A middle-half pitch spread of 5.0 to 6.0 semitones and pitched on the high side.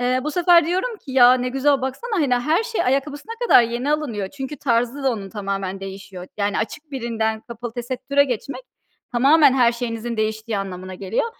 No: average, 4.5 semitones; high, 245 Hz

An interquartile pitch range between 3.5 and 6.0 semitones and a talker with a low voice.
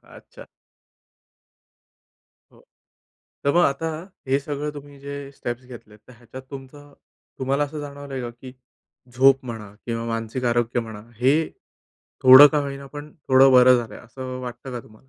No: average, 2.8 semitones; low, 130 Hz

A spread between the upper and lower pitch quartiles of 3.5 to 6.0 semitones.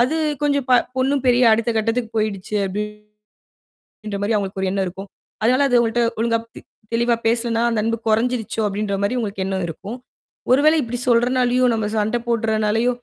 No: average, 2.7 semitones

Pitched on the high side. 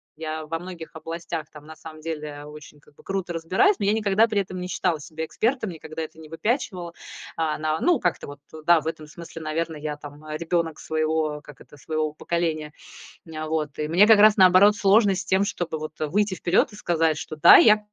No: medium, 160 Hz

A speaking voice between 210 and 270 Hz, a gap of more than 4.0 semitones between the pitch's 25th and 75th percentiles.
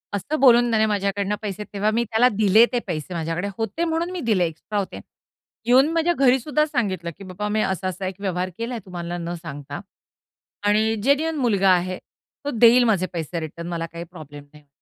No: high, 200 Hz; average, 5.3 semitones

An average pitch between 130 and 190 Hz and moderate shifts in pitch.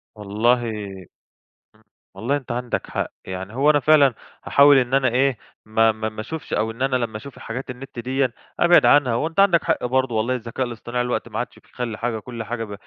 No: low, 120 Hz; average, 3.3 semitones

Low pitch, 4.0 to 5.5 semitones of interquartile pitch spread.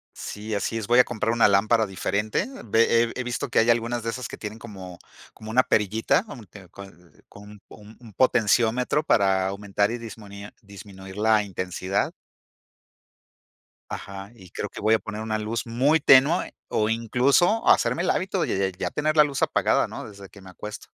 No: low, 110 Hz; average, 3.1 semitones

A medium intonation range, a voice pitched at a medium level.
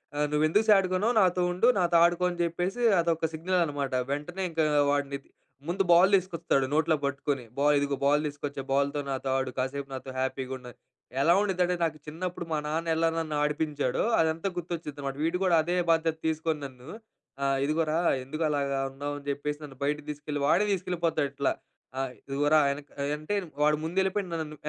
Yes: average, 3.3 semitones; medium, 155 Hz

